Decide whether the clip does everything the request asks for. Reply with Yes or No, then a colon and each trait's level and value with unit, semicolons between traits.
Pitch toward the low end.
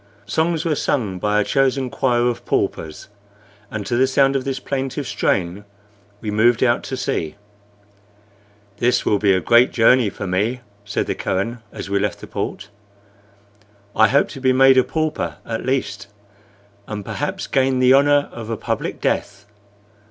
Yes: low, 120 Hz